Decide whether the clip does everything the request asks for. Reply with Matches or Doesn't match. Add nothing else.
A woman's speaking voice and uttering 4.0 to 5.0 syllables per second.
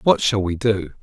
Doesn't match